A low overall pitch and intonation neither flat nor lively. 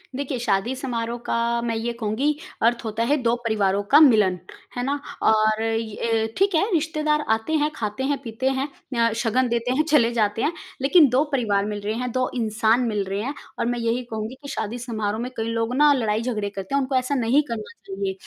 No: high, 230 Hz; average, 3.3 semitones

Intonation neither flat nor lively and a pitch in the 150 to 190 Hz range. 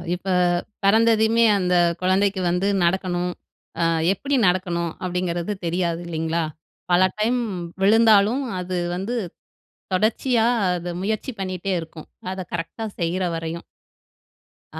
Yes: average, 3.7 semitones; medium, 185 Hz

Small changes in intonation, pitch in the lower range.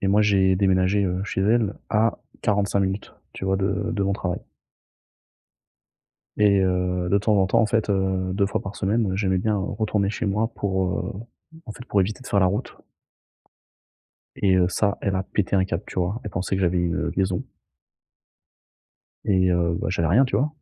Yes: narrow, 1.8 semitones; very low, 95 Hz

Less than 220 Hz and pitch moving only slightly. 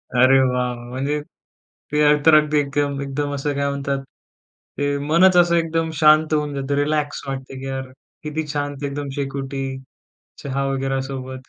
Yes: medium, 140 Hz; narrow, 1.8 semitones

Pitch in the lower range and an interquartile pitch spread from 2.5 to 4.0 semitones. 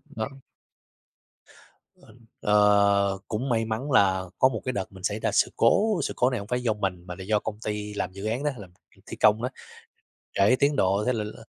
Yes: low, 105 Hz; average, 3.7 semitones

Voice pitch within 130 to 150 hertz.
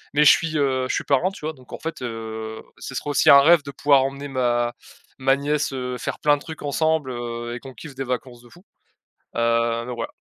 Yes: low, 135 Hz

